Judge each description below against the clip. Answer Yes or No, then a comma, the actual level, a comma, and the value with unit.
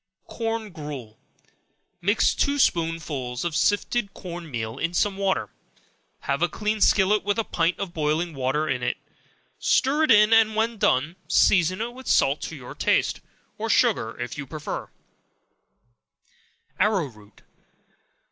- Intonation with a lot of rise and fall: Yes, wide, 6.3 semitones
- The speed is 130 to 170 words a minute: Yes, average, 145 wpm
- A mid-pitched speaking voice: Yes, medium, 175 Hz